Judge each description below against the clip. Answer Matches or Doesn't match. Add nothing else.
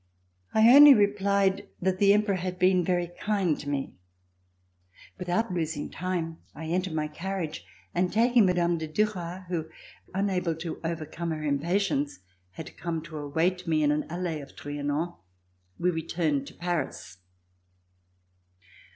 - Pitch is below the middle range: Doesn't match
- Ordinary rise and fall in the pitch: Matches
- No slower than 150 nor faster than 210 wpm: Doesn't match